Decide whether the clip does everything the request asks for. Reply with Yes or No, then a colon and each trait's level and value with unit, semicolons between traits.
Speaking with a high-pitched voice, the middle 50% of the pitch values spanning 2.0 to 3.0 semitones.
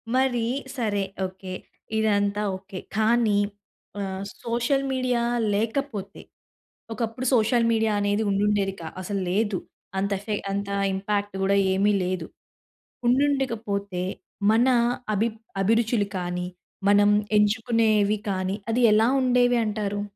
Yes: high, 210 Hz; narrow, 2.6 semitones